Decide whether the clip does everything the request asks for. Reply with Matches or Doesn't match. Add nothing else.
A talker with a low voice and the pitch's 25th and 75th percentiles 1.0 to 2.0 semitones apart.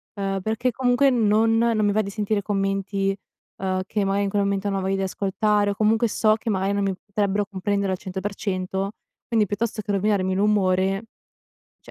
Doesn't match